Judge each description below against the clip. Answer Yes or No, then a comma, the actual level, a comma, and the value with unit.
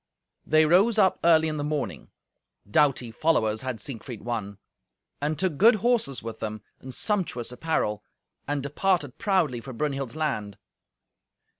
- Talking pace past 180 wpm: No, average, 140 wpm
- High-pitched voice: No, medium, 145 Hz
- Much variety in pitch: Yes, wide, 5.9 semitones